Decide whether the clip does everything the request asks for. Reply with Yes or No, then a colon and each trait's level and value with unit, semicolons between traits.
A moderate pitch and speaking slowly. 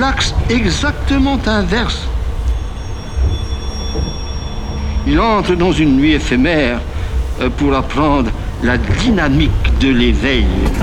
No: very low, 90 Hz; slow, 85 wpm